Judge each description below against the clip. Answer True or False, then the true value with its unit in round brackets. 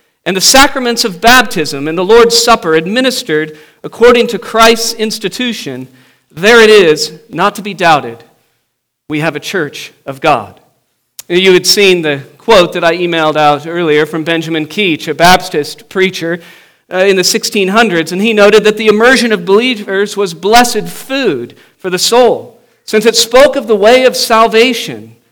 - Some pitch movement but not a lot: False (5.9 semitones)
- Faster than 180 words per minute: False (165 wpm)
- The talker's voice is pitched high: True (200 Hz)